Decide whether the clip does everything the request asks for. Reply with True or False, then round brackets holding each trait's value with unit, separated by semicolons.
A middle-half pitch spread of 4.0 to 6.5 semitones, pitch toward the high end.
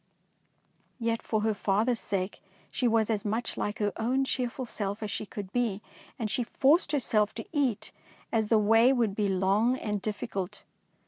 False (2.7 semitones; 220 Hz)